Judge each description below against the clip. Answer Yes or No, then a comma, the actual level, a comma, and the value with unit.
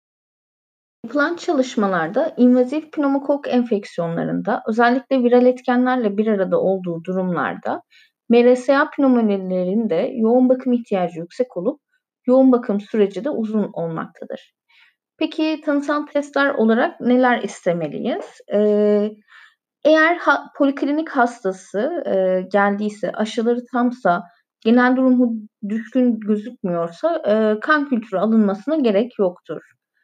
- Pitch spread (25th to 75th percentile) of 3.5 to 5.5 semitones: Yes, average, 4.9 semitones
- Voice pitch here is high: Yes, high, 240 Hz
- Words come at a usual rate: No, slow, 90 wpm